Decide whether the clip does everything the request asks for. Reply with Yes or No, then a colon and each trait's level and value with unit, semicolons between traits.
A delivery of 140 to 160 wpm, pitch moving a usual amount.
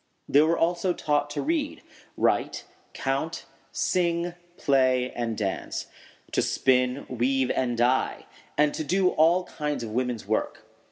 Yes: average, 145 wpm; average, 5.0 semitones